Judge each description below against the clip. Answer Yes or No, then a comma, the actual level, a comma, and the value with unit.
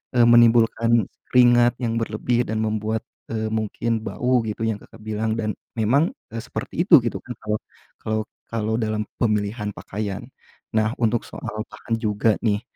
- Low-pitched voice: Yes, low, 110 Hz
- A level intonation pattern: Yes, narrow, 1.6 semitones